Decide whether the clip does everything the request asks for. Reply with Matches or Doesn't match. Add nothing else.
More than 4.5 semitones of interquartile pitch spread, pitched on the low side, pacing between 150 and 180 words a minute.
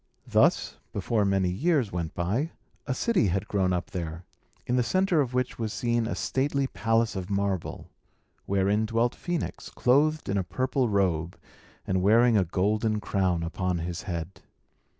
Matches